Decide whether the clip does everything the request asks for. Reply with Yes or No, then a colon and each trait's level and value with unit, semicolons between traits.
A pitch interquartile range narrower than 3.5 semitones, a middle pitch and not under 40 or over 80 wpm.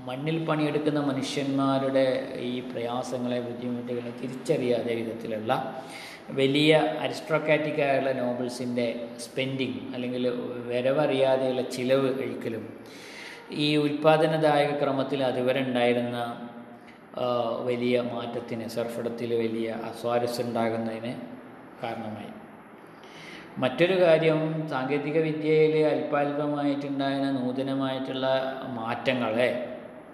No: average, 2.9 semitones; low, 130 Hz; average, 65 wpm